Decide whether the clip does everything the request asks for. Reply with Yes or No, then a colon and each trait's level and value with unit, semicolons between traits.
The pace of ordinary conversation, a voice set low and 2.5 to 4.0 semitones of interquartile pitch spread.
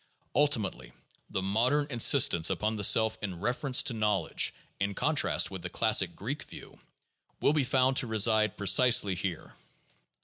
No: average, 160 wpm; low, 110 Hz; average, 4.7 semitones